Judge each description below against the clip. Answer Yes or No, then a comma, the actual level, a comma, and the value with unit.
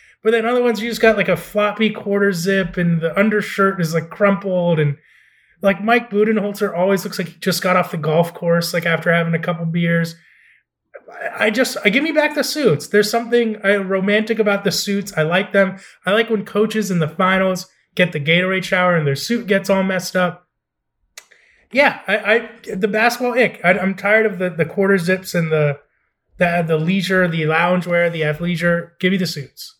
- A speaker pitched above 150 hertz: Yes, high, 190 Hz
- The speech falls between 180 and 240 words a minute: Yes, fast, 205 wpm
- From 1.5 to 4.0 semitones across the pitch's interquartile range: Yes, average, 3.5 semitones